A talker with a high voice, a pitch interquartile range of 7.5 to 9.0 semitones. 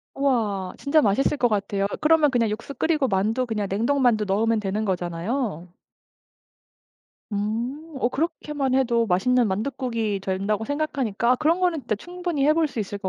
No: high, 235 Hz; wide, 5.4 semitones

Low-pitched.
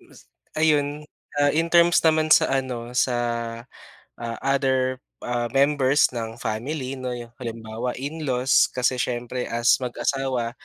Yes: low, 130 Hz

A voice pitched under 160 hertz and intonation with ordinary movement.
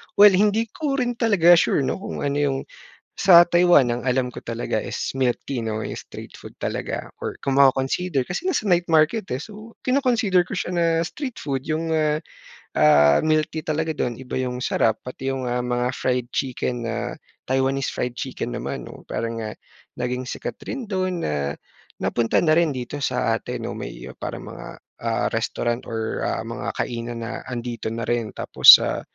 No: low, 135 Hz; wide, 6.1 semitones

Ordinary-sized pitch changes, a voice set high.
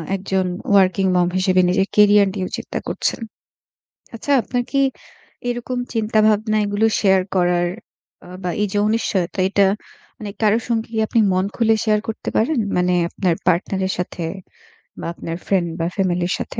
Yes: average, 3.0 semitones; high, 195 Hz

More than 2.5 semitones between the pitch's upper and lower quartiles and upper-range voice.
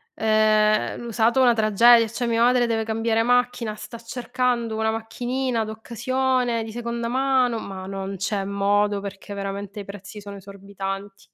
Yes: average, 2.9 semitones; high, 220 Hz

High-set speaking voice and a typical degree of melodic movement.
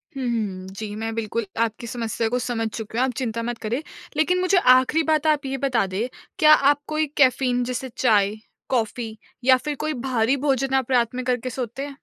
Yes: very high, 250 Hz; average, 3.1 semitones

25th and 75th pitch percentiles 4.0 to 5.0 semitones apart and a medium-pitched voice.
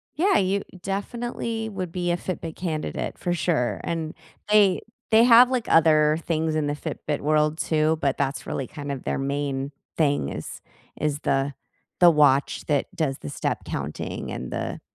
Yes: average, 4.4 semitones; medium, 155 Hz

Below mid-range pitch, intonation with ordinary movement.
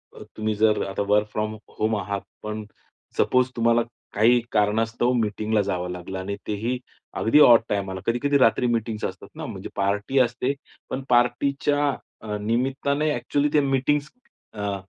Yes: low, 115 Hz; average, 3.6 semitones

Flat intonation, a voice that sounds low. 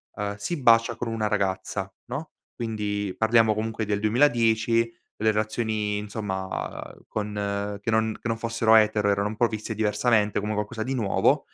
Yes: narrow, 1.8 semitones; low, 110 Hz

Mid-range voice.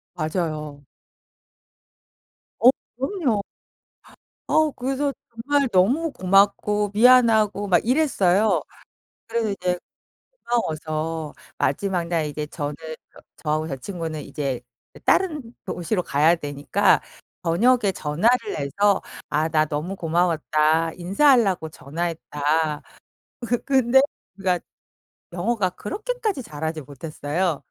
Yes: medium, 180 Hz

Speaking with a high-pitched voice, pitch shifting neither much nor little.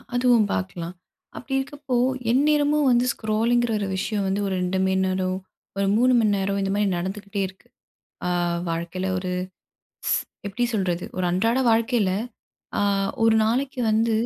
Yes: high, 205 Hz; average, 4.2 semitones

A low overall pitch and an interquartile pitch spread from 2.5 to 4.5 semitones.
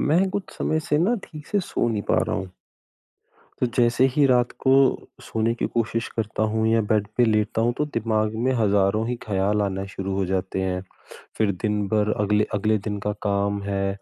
Yes: low, 110 Hz; average, 2.9 semitones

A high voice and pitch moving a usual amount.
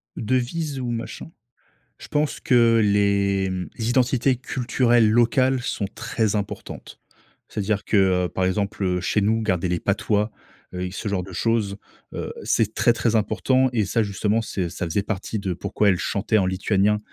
No: low, 105 Hz; average, 3.2 semitones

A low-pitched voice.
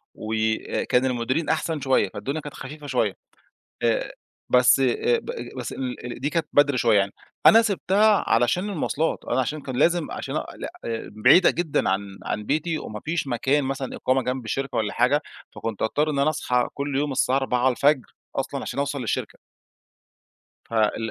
Yes: low, 130 Hz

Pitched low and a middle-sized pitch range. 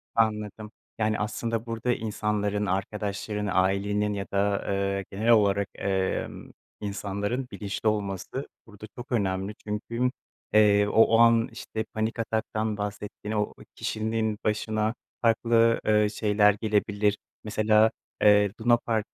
No: low, 105 Hz; narrow, 1.5 semitones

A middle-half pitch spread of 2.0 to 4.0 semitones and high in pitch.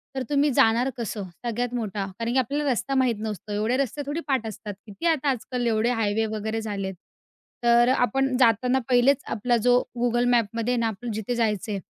Yes: average, 2.8 semitones; high, 235 Hz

